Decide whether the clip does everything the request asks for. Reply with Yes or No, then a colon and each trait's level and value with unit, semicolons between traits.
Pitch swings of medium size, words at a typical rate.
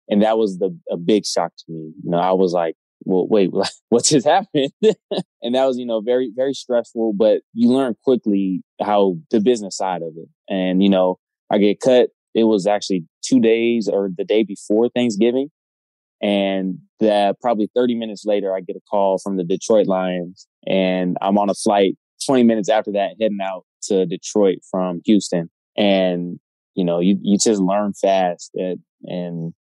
Yes: average, 3.8 semitones; average, 185 wpm